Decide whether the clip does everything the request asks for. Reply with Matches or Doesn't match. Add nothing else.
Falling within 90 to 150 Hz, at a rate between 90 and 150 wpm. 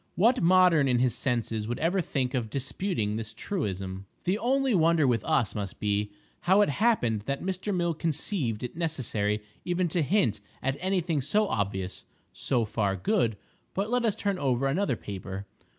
Doesn't match